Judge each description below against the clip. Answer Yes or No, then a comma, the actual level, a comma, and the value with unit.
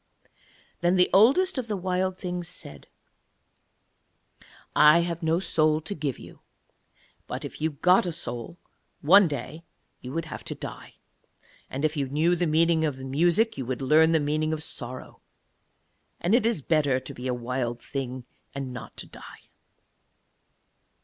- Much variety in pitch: No, average, 4.5 semitones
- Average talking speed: Yes, average, 160 wpm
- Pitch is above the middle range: No, medium, 155 Hz